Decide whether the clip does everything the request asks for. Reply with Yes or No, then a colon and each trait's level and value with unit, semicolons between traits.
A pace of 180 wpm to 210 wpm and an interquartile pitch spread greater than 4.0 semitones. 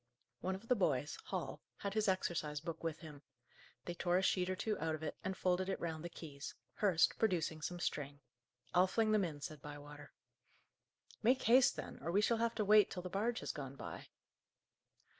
Yes: average, 200 wpm; average, 4.6 semitones